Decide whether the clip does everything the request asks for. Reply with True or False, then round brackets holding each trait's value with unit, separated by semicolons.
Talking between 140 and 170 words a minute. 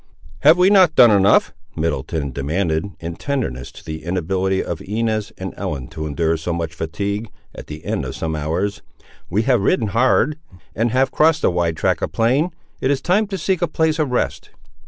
False (195 wpm)